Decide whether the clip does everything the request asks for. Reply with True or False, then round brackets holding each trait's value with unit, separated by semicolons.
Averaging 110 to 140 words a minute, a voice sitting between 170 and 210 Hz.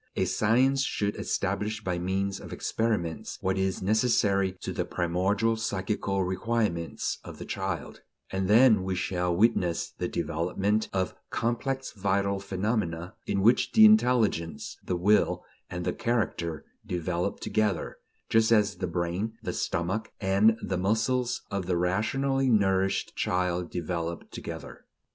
False (135 wpm; 100 Hz)